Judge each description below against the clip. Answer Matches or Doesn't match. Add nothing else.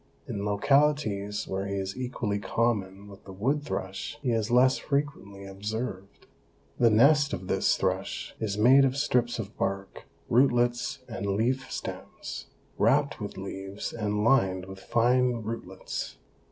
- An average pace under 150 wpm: Matches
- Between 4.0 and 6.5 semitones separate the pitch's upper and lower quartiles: Matches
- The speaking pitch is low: Matches